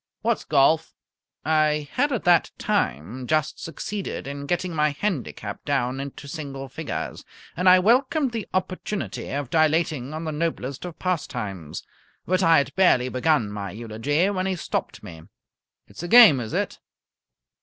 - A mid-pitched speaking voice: Yes, medium, 155 Hz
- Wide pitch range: Yes, wide, 5.7 semitones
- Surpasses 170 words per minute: No, average, 155 wpm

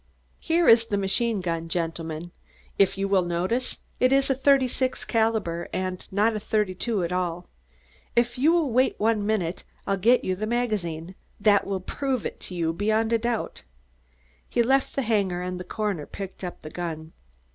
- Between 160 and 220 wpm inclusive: Yes, average, 180 wpm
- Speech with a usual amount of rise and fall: Yes, average, 4.8 semitones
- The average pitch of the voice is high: Yes, high, 205 Hz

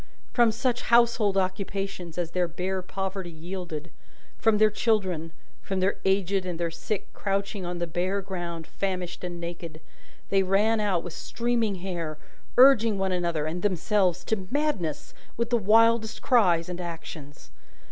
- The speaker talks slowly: No, average, 150 wpm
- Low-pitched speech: No, high, 190 Hz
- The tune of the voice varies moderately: Yes, average, 3.5 semitones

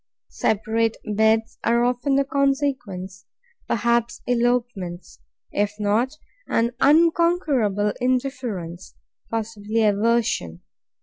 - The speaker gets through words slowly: Yes, slow, 80 wpm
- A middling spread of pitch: Yes, average, 3.8 semitones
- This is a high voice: Yes, high, 230 Hz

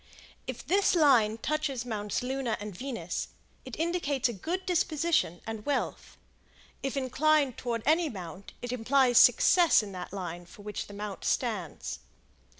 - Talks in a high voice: Yes, high, 245 Hz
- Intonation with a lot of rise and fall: Yes, wide, 6.3 semitones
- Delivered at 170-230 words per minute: No, average, 150 wpm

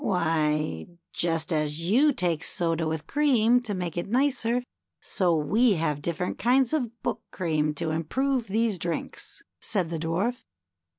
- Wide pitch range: Yes, wide, 6.8 semitones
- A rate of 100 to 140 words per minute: No, average, 150 wpm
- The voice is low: No, medium, 180 Hz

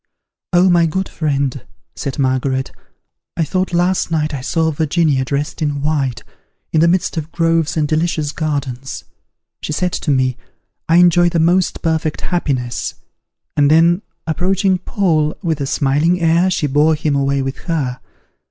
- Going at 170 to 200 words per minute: No, average, 155 wpm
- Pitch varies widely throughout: No, average, 3.4 semitones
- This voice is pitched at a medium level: Yes, medium, 155 Hz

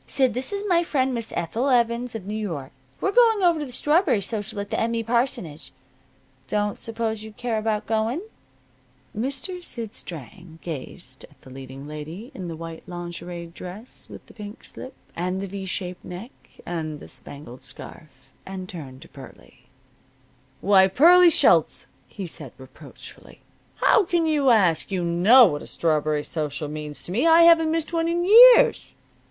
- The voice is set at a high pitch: Yes, high, 210 Hz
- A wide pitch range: Yes, wide, 7.7 semitones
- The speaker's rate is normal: Yes, average, 175 wpm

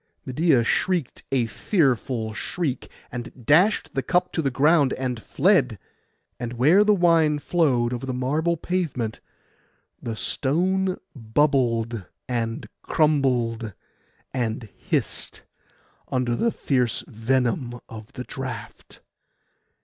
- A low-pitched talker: Yes, low, 130 Hz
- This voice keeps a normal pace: No, slow, 110 wpm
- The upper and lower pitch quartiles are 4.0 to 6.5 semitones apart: Yes, average, 5.3 semitones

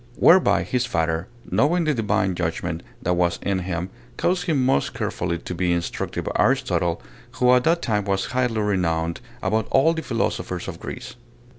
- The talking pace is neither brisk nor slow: Yes, average, 170 wpm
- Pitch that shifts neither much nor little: No, wide, 6.5 semitones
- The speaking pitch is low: Yes, low, 100 Hz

